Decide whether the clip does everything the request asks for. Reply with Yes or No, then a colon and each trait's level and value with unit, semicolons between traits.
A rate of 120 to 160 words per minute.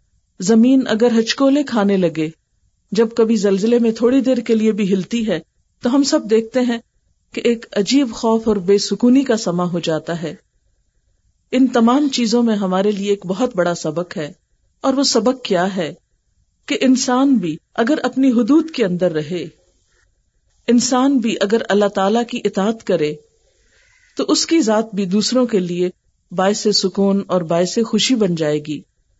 No: average, 170 wpm